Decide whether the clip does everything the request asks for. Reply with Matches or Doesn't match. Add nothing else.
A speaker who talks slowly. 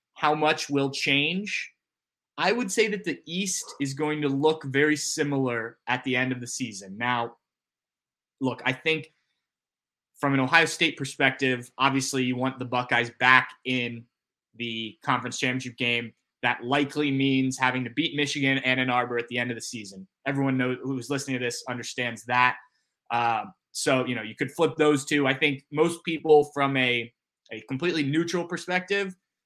Doesn't match